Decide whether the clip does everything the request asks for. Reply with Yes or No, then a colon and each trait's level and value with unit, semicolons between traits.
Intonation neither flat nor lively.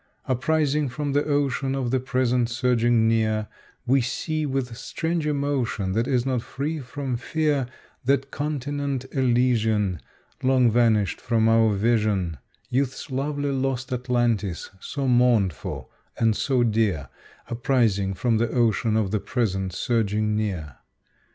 Yes: average, 3.6 semitones